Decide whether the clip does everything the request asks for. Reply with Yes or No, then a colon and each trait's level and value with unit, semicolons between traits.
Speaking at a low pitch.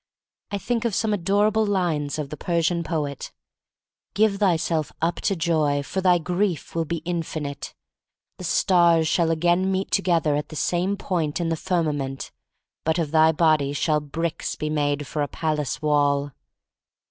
No: medium, 165 Hz